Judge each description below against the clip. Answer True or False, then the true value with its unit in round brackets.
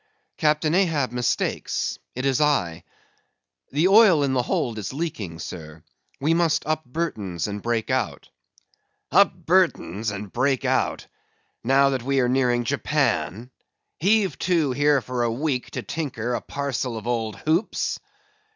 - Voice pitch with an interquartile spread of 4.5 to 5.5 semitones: True (5.2 semitones)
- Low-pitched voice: True (130 Hz)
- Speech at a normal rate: True (145 wpm)